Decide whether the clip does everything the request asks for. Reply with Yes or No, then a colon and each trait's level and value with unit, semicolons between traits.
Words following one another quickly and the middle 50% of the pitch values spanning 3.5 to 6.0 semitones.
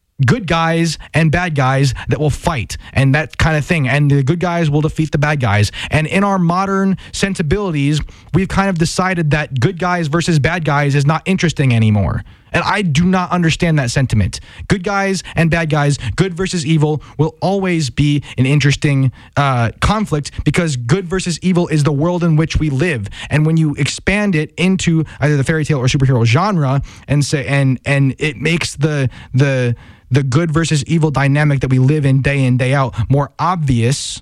No: average, 195 wpm; average, 4.1 semitones